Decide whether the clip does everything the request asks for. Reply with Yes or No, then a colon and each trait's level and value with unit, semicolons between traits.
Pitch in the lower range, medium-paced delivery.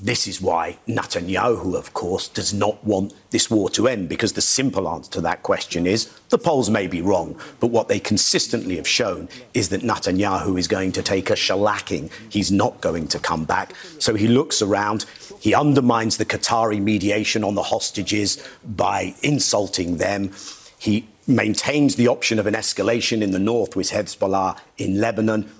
Yes: low, 105 Hz; average, 180 wpm